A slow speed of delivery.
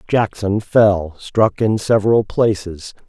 Yes: slow, 115 wpm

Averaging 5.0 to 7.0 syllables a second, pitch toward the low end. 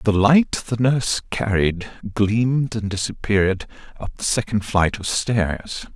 No: 4.1 syllables/s; low, 105 Hz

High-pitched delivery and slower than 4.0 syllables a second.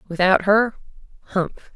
No: high, 195 Hz; 4.1 syllables/s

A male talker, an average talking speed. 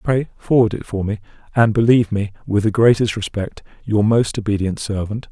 Yes: male; average, 180 wpm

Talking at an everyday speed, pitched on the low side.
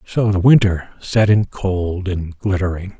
Yes: average, 160 wpm; very low, 95 Hz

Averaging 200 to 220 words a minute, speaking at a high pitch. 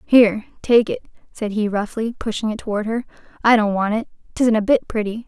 Yes: fast, 205 wpm; high, 225 Hz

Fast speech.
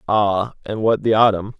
No: average, 190 wpm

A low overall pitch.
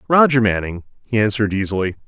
Yes: low, 110 Hz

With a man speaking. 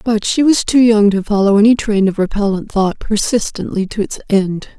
No: female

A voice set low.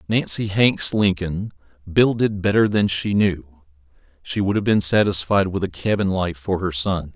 Yes: very low, 95 Hz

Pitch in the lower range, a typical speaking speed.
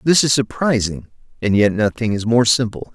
Yes: low, 115 Hz; average, 185 wpm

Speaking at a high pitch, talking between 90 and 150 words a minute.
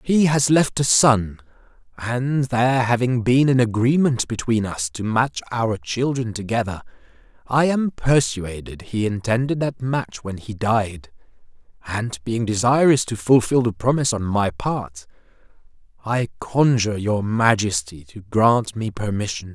No: low, 115 Hz; average, 140 wpm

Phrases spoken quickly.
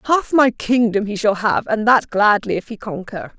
Yes: fast, 215 wpm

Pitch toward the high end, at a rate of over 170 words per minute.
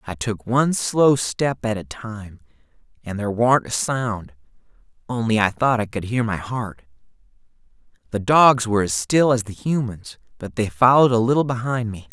No: low, 115 Hz; average, 180 wpm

